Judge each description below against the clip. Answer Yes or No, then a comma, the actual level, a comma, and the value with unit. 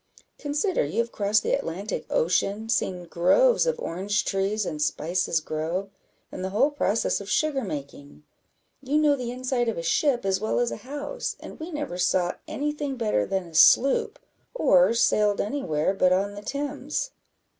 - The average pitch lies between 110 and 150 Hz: No, high, 210 Hz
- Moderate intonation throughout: No, wide, 7.4 semitones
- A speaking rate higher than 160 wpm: Yes, average, 175 wpm